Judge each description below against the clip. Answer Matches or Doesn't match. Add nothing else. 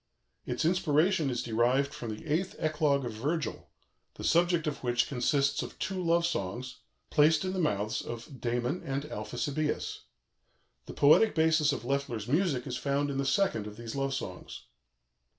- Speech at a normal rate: Matches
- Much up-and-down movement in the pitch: Doesn't match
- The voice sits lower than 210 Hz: Matches